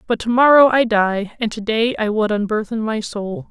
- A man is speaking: No, female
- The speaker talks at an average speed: Yes, average, 190 wpm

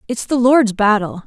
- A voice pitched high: Yes, high, 225 Hz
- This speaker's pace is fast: No, average, 190 wpm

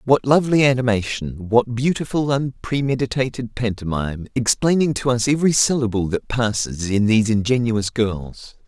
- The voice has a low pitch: Yes, low, 120 Hz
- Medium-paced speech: No, slow, 125 wpm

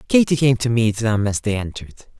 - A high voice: No, low, 120 Hz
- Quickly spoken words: Yes, fast, 220 wpm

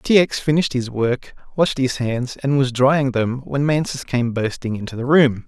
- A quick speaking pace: Yes, fast, 210 wpm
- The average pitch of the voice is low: Yes, low, 130 Hz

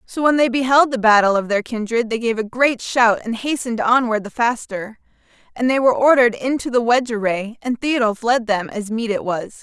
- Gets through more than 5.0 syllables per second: Yes, 5.5 syllables/s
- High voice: Yes, high, 235 Hz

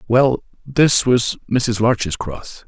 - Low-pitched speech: Yes, low, 120 Hz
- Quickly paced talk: No, slow, 135 wpm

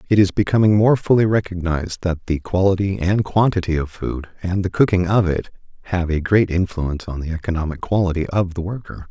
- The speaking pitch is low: Yes, very low, 90 Hz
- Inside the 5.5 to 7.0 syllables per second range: Yes, 5.7 syllables/s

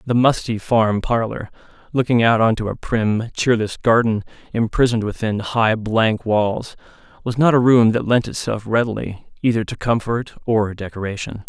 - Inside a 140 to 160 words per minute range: Yes, average, 155 wpm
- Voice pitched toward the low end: Yes, low, 115 Hz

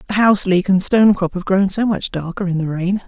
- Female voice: Yes, female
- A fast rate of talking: Yes, fast, 275 wpm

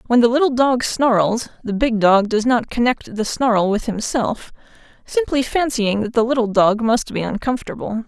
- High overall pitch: Yes, high, 230 Hz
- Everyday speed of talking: Yes, average, 180 wpm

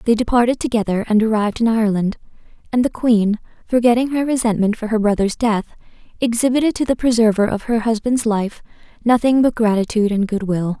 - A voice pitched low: No, high, 225 Hz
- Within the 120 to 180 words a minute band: Yes, average, 170 wpm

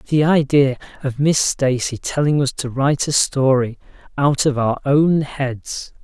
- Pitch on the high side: No, low, 135 Hz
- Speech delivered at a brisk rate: No, average, 160 wpm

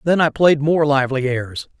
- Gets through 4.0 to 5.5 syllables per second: Yes, 5.0 syllables/s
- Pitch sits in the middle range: Yes, medium, 145 Hz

